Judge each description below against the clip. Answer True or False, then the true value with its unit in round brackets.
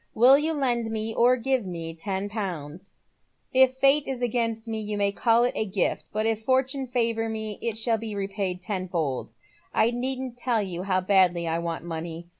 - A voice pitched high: True (220 Hz)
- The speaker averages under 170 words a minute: False (190 wpm)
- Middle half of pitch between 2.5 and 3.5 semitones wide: False (4.7 semitones)